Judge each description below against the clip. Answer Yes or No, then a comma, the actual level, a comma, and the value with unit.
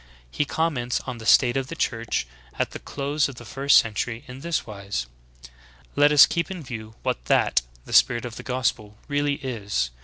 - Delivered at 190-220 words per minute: Yes, average, 195 wpm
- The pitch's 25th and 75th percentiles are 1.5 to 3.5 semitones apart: No, average, 4.2 semitones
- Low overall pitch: Yes, low, 125 Hz